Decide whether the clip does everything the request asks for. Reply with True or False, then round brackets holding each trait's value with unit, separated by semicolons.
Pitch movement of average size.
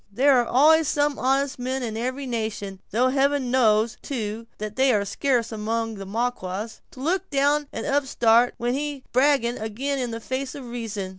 True (3.6 semitones)